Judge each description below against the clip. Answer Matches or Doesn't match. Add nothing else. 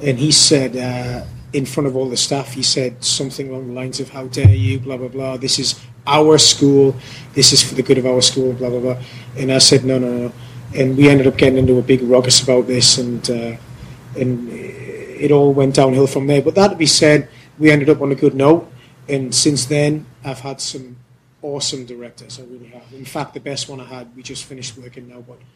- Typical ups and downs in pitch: Doesn't match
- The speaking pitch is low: Matches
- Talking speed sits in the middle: Doesn't match